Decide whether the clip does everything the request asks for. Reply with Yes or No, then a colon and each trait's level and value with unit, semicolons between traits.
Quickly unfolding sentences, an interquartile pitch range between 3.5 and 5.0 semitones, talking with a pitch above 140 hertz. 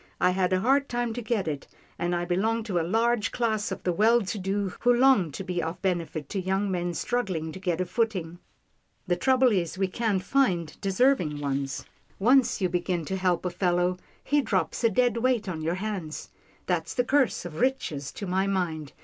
Yes: fast, 210 wpm; average, 4.7 semitones; high, 190 Hz